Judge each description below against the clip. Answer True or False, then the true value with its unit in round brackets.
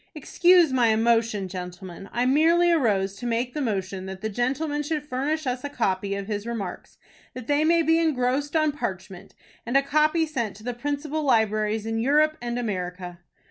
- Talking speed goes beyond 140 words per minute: True (180 wpm)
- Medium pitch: False (245 Hz)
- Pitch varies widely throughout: True (6.3 semitones)